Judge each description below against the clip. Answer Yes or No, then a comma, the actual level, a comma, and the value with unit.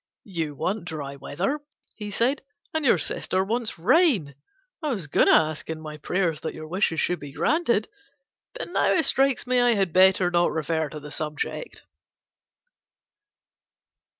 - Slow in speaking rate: No, average, 160 wpm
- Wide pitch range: Yes, wide, 7.1 semitones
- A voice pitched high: No, medium, 180 Hz